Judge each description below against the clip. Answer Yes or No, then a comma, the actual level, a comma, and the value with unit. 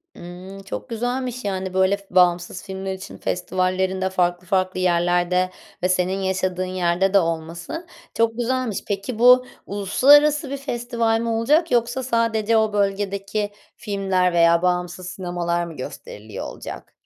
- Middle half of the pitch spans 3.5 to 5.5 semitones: Yes, average, 4.1 semitones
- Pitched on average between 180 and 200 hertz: Yes, high, 190 Hz